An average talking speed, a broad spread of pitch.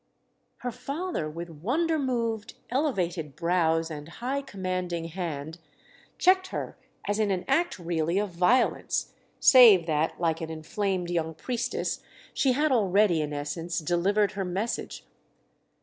No: slow, 130 wpm; wide, 6.4 semitones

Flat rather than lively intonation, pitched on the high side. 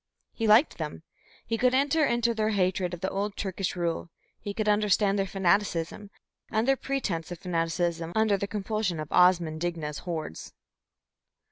No: average, 3.9 semitones; high, 195 Hz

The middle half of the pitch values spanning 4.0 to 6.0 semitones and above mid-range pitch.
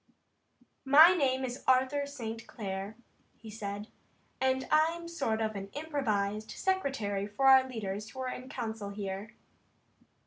Yes: average, 4.7 semitones; high, 235 Hz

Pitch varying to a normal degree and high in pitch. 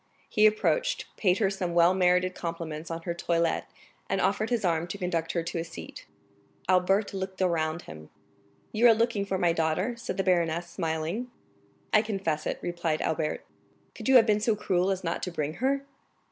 No: average, 3.8 semitones; medium, 180 Hz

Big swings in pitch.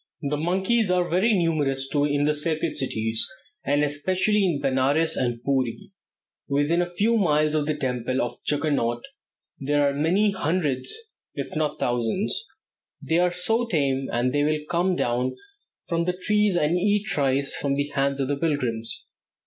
No: average, 4.5 semitones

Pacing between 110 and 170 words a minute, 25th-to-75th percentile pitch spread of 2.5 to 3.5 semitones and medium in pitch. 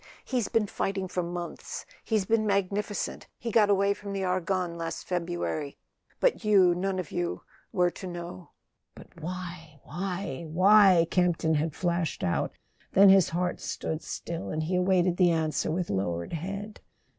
Yes: average, 155 wpm; average, 2.8 semitones; medium, 180 Hz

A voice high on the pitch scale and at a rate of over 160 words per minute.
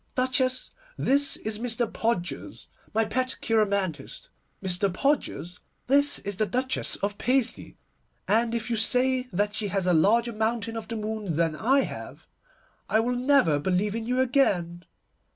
No: high, 225 Hz; average, 150 wpm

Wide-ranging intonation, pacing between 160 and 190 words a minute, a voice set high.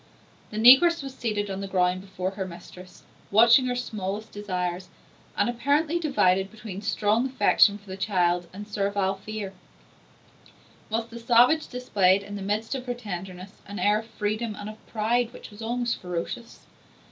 No: average, 3.6 semitones; average, 165 wpm; high, 210 Hz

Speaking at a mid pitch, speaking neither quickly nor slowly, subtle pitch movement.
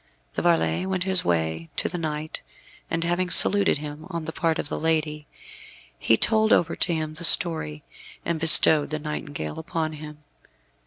Yes: medium, 160 Hz; average, 170 wpm; narrow, 2.2 semitones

